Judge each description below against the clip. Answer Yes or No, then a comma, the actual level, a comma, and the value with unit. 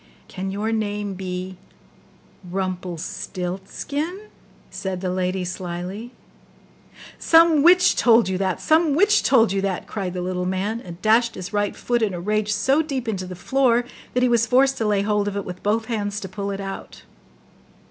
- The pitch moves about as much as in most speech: Yes, average, 4.2 semitones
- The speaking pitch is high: Yes, high, 205 Hz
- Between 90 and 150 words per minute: No, average, 175 wpm